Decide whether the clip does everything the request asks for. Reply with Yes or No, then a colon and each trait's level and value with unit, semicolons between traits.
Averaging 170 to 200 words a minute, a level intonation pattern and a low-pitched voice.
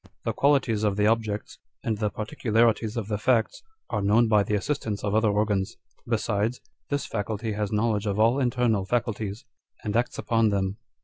Yes: average, 175 wpm; narrow, 2.0 semitones; low, 110 Hz